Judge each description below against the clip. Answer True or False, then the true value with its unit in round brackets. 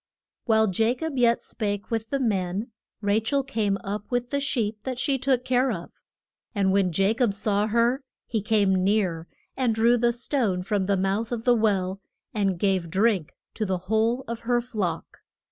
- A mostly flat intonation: False (3.6 semitones)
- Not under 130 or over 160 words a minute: False (185 wpm)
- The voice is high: True (220 Hz)